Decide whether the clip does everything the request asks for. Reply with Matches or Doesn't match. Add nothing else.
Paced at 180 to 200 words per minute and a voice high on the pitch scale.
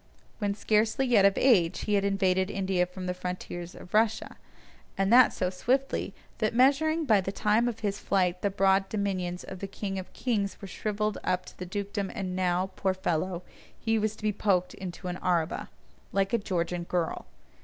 Matches